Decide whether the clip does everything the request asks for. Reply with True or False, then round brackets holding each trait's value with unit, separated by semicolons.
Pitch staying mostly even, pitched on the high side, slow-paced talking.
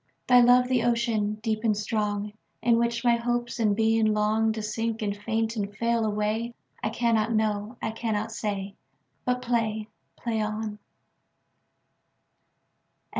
True (1.8 semitones; 220 Hz; 125 wpm)